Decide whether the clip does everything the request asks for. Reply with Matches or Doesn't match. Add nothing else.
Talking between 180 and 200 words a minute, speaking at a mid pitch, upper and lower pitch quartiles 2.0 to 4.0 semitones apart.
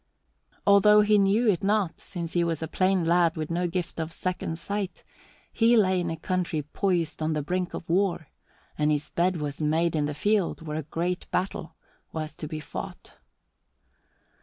Matches